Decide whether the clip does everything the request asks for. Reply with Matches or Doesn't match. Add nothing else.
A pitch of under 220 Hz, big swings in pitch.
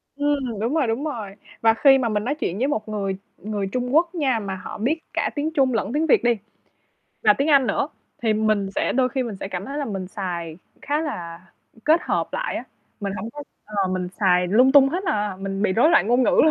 Doesn't match